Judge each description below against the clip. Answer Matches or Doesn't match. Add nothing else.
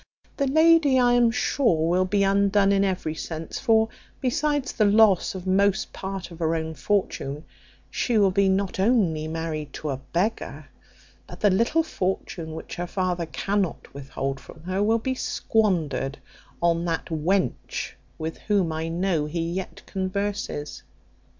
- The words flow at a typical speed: Matches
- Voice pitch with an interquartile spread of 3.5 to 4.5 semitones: Matches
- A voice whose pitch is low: Doesn't match